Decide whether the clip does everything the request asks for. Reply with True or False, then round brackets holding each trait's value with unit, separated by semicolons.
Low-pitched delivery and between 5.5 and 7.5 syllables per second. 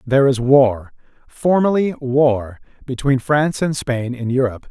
False (130 Hz; 4.6 syllables/s)